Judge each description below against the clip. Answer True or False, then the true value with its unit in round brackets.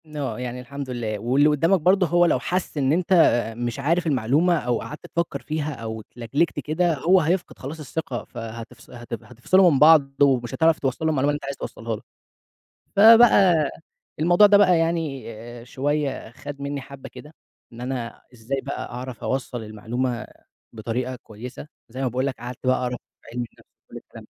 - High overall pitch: False (135 Hz)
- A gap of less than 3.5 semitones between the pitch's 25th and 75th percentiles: False (4.7 semitones)